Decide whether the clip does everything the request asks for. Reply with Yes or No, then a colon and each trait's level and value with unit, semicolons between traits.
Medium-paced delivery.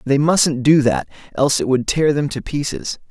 No: fast, 215 wpm